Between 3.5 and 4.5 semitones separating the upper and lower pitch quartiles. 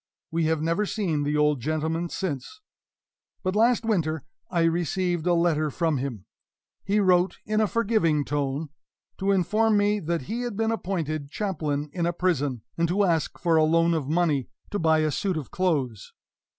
Yes: average, 4.1 semitones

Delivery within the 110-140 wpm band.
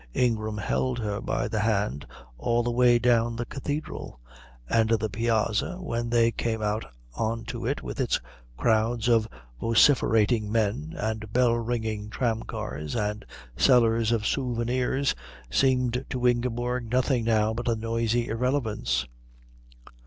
Yes: slow, 135 wpm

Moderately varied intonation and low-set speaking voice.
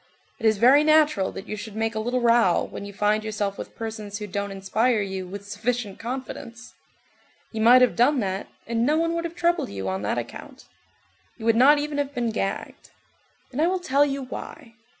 No: average, 4.8 semitones; high, 230 Hz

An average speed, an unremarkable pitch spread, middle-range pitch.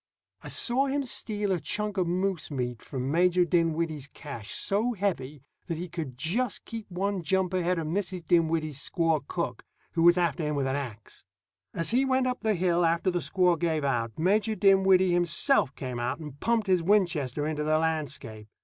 Yes: average, 185 wpm; average, 4.3 semitones; medium, 170 Hz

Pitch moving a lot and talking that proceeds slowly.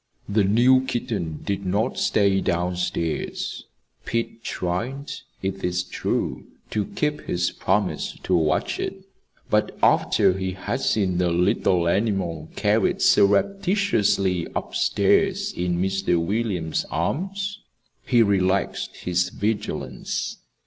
No: average, 4.2 semitones; slow, 115 wpm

